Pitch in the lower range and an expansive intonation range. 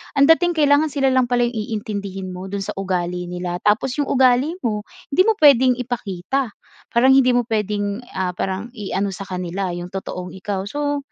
No: high, 210 Hz; wide, 5.7 semitones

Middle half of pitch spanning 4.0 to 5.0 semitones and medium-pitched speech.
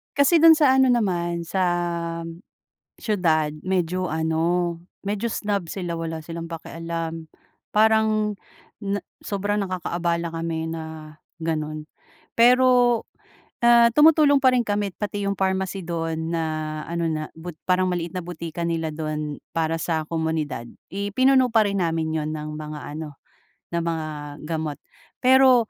Yes: average, 4.4 semitones; medium, 170 Hz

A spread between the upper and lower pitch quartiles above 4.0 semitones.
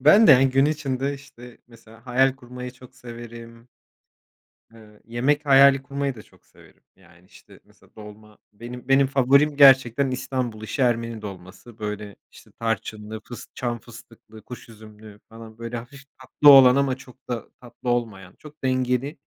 No: average, 3.1 semitones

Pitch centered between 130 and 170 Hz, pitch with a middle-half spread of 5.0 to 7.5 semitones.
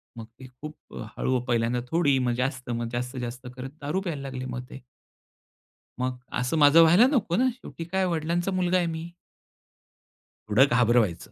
Yes: low, 135 Hz; average, 5.3 semitones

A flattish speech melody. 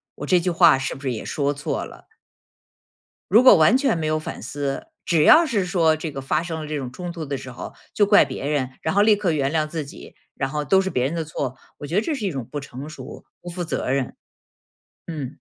No: average, 4.2 semitones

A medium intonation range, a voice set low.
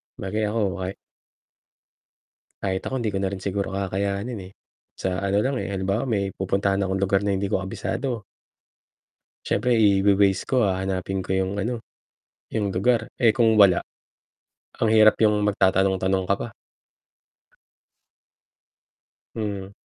No: narrow, 2.0 semitones; low, 100 Hz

